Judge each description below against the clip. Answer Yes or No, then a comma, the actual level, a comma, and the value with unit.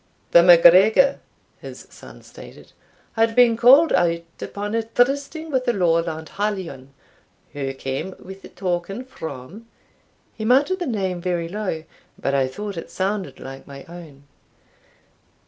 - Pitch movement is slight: No, wide, 5.5 semitones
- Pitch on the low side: No, high, 190 Hz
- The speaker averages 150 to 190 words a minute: No, average, 140 wpm